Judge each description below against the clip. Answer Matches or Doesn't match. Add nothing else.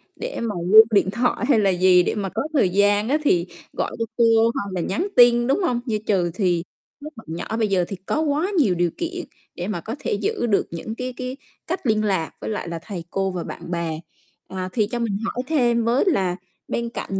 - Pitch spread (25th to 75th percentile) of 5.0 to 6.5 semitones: Doesn't match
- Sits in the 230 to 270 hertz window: Doesn't match